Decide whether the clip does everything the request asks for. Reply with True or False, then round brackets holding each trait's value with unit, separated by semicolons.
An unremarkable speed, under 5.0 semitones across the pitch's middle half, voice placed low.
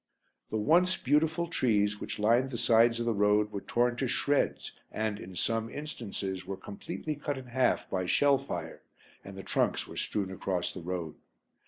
False (180 wpm; 5.3 semitones; 110 Hz)